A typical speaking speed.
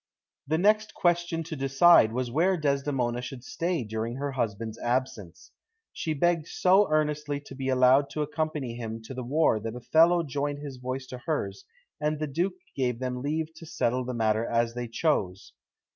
Yes: average, 175 wpm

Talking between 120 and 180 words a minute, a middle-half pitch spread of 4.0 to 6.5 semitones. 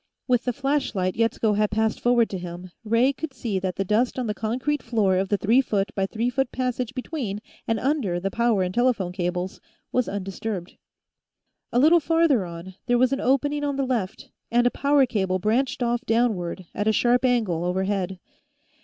No: average, 190 wpm; average, 4.8 semitones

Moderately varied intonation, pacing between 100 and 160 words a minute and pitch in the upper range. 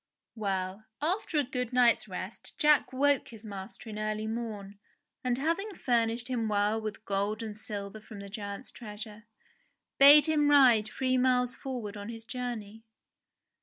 Yes: average, 3.5 semitones; average, 155 wpm; high, 225 Hz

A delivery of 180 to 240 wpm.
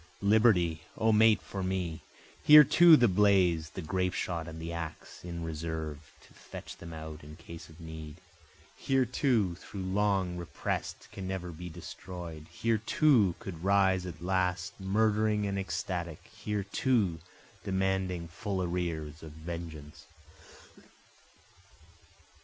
No: slow, 135 wpm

